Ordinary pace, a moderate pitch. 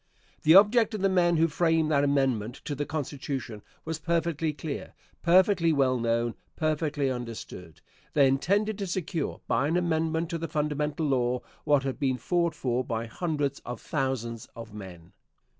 Yes: average, 160 wpm; medium, 150 Hz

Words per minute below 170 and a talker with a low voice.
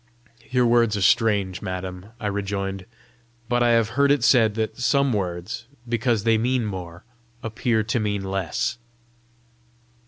Yes: average, 145 wpm; low, 110 Hz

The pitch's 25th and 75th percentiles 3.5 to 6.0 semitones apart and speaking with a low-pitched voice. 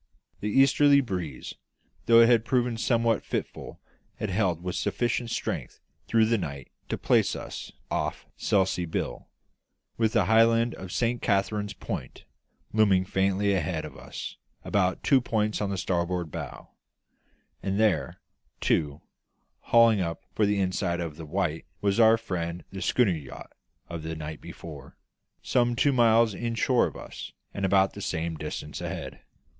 Yes: average, 4.9 semitones; low, 100 Hz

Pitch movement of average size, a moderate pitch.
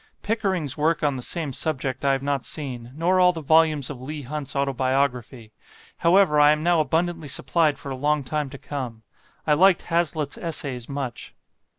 Yes: average, 3.3 semitones; medium, 145 Hz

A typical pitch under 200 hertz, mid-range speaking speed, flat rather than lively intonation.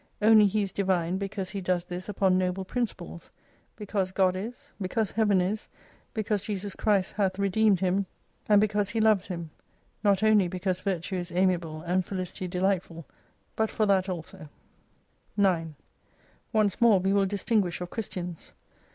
Yes: high, 190 Hz; average, 160 wpm; narrow, 2.3 semitones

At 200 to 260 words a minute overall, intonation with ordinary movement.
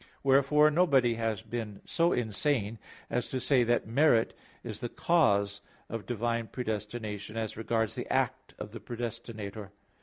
No: average, 145 wpm; average, 3.0 semitones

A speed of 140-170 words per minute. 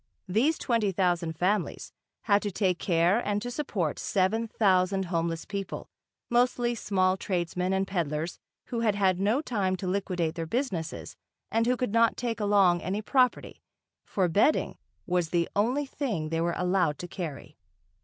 Yes: average, 160 wpm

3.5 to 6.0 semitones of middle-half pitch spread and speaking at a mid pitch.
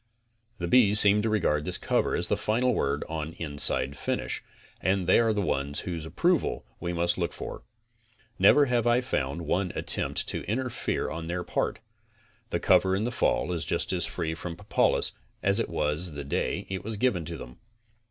No: average, 5.0 semitones; very low, 90 Hz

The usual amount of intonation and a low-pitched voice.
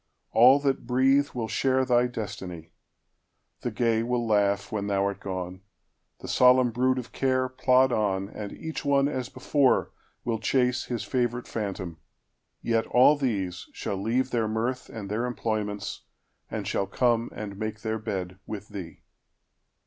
Yes: average, 3.9 semitones; low, 115 Hz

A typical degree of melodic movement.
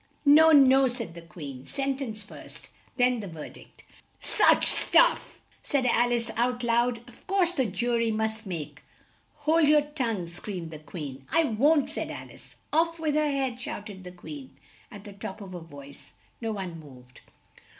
No: wide, 7.2 semitones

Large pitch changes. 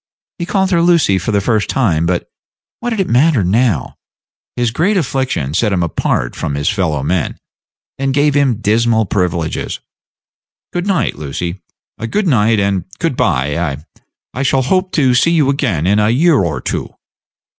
Yes: wide, 8.5 semitones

